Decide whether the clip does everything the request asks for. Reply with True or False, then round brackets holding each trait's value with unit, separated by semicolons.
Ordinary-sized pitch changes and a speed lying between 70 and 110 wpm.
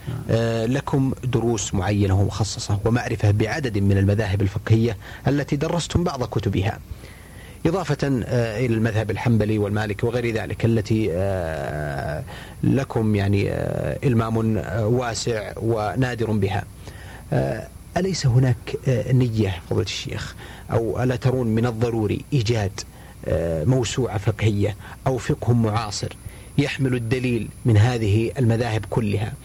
True (3.2 semitones; 100 wpm)